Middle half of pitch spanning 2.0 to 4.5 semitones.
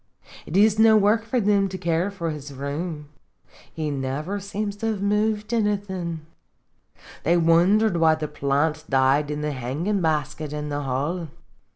No: wide, 5.4 semitones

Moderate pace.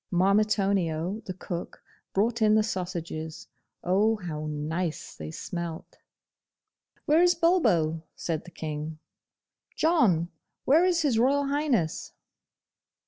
No: slow, 110 wpm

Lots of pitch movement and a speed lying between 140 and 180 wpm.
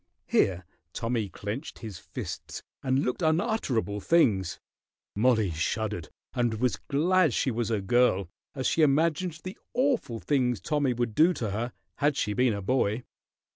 Yes: wide, 6.0 semitones; average, 150 wpm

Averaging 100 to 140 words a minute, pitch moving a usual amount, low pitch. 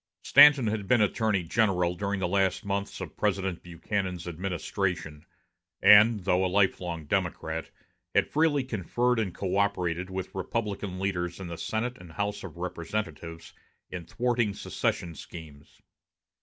Yes: slow, 135 wpm; average, 3.1 semitones; very low, 95 Hz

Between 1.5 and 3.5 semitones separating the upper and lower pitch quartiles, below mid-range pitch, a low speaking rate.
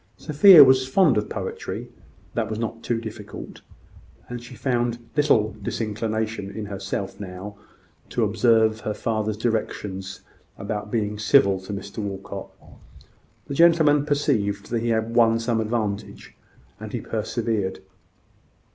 Yes: average, 2.8 semitones; low, 110 Hz; slow, 130 wpm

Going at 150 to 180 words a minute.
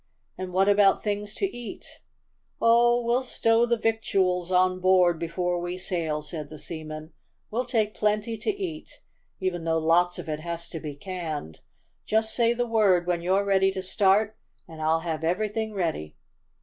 Yes: average, 170 wpm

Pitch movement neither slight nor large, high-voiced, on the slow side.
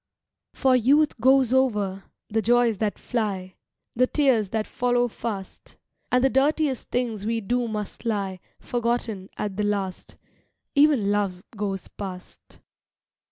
Yes: average, 3.8 semitones; high, 225 Hz; slow, 130 wpm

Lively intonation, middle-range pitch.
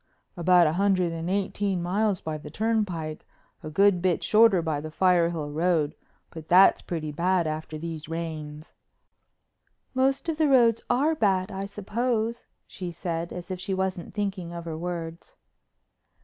No: average, 3.7 semitones; medium, 180 Hz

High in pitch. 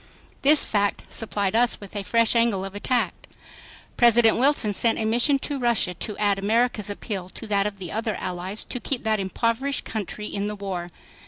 Yes: high, 215 Hz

